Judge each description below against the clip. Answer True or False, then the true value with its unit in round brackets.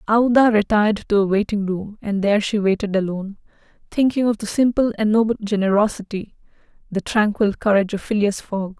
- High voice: True (210 Hz)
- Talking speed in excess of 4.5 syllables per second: True (6.0 syllables/s)